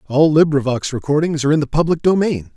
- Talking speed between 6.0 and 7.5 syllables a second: Yes, 6.3 syllables/s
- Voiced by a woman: No, male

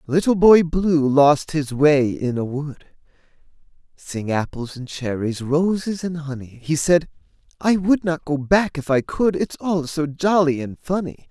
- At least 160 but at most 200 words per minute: Yes, average, 170 wpm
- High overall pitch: No, medium, 155 Hz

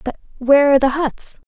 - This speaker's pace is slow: No, fast, 205 wpm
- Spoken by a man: No, female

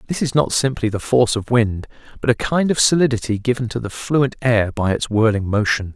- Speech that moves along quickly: Yes, fast, 220 wpm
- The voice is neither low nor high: No, low, 120 Hz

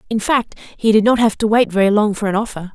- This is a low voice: No, high, 215 Hz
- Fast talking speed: Yes, fast, 285 wpm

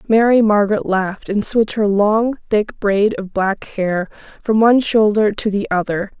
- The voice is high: Yes, high, 210 Hz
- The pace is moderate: Yes, average, 175 wpm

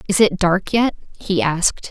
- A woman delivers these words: Yes, female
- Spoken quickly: No, average, 190 wpm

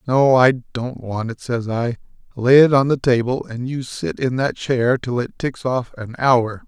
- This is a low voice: Yes, low, 125 Hz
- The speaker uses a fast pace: Yes, fast, 215 wpm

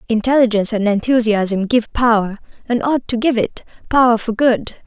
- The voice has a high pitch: Yes, high, 230 Hz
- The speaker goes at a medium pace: Yes, average, 150 wpm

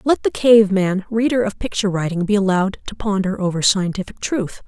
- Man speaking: No, female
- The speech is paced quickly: No, average, 190 wpm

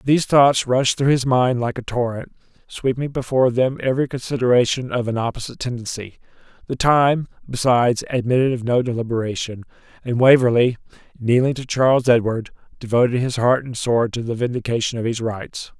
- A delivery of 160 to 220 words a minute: No, average, 150 wpm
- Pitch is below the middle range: Yes, low, 125 Hz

